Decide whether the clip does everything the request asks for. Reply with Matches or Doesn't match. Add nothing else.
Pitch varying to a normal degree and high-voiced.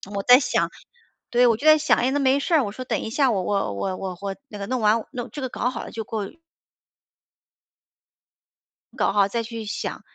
Matches